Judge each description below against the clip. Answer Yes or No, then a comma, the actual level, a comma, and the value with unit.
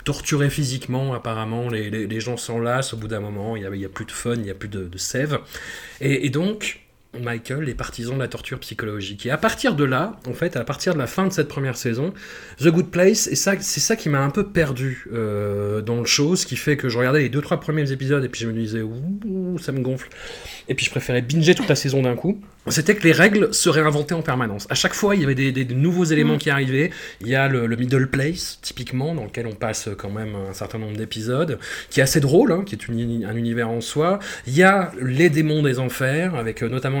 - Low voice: Yes, low, 130 Hz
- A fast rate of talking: Yes, fast, 260 wpm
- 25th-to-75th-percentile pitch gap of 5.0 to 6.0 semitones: Yes, wide, 5.4 semitones